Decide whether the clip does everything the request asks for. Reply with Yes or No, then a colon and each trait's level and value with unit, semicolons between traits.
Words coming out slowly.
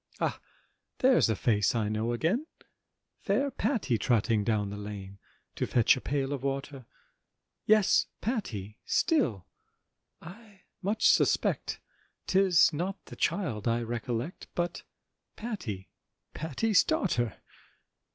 Yes: slow, 115 wpm